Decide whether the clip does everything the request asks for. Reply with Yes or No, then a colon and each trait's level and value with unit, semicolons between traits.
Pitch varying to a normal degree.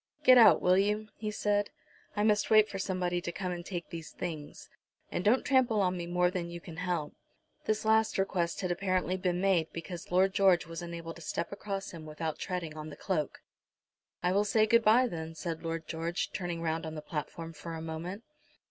Yes: average, 3.1 semitones